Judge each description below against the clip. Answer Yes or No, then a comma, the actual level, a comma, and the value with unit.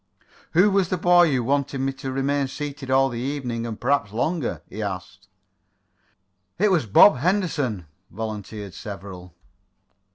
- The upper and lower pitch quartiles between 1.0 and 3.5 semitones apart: No, average, 5.3 semitones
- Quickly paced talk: No, average, 140 wpm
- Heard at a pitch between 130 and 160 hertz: Yes, low, 135 Hz